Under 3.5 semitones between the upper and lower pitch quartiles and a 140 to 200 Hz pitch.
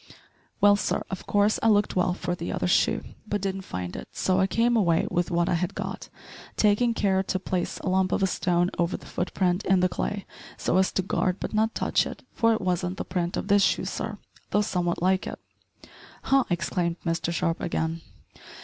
Yes: narrow, 2.5 semitones; medium, 185 Hz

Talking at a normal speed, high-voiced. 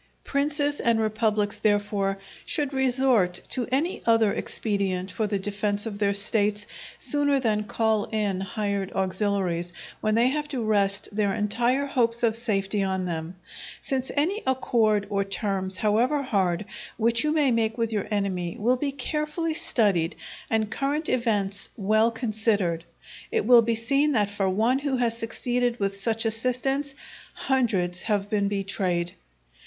Yes: average, 150 wpm; high, 220 Hz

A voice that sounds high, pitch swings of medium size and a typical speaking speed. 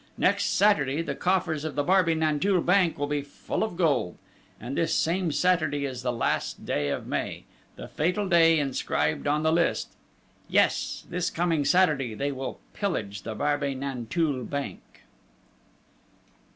No: medium, 150 Hz; average, 4.1 semitones; average, 150 wpm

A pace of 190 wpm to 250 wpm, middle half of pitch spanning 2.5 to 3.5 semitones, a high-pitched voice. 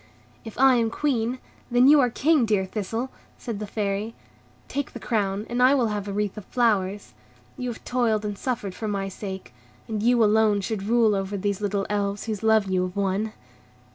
Yes: average, 200 wpm; average, 3.0 semitones; high, 215 Hz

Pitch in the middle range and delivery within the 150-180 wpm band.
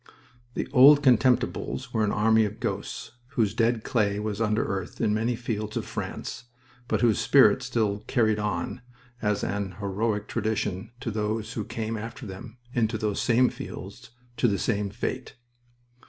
No: low, 110 Hz; average, 160 wpm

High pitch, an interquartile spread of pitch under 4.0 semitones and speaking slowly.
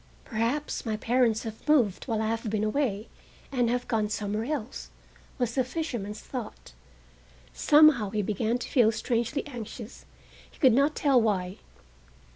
No: high, 230 Hz; average, 3.3 semitones; average, 150 wpm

